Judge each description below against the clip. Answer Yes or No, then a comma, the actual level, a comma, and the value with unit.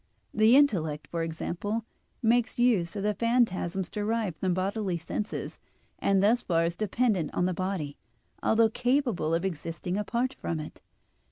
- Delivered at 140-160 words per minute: Yes, average, 155 wpm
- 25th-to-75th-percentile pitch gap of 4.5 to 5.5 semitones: Yes, average, 5.1 semitones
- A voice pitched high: Yes, high, 195 Hz